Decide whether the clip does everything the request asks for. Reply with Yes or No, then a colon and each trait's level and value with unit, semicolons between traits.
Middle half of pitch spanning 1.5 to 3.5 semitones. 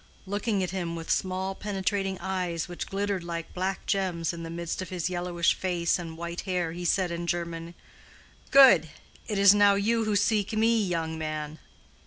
Yes: average, 2.7 semitones